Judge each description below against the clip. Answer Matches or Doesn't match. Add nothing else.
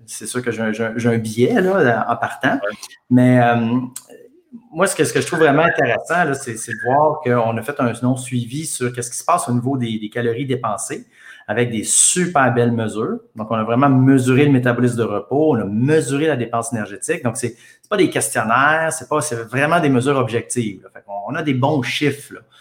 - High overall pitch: Doesn't match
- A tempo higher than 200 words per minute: Matches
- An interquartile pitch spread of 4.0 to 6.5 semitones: Doesn't match